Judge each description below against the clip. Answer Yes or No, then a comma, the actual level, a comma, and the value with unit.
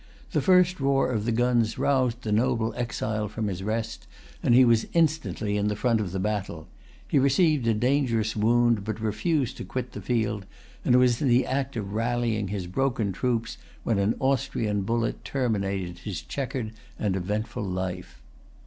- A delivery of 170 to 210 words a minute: Yes, average, 175 wpm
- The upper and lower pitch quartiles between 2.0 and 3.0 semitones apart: No, average, 3.5 semitones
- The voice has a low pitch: Yes, low, 115 Hz